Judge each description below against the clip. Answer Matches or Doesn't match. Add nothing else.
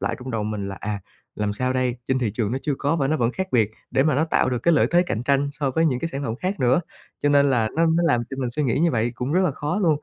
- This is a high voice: Doesn't match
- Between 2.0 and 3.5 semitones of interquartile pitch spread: Doesn't match